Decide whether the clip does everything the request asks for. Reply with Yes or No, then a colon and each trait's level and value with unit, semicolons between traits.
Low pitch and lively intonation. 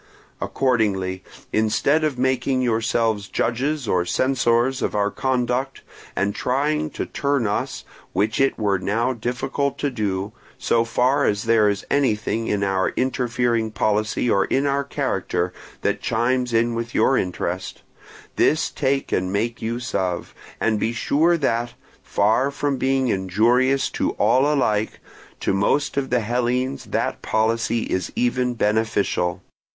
No: low, 120 Hz; average, 3.8 semitones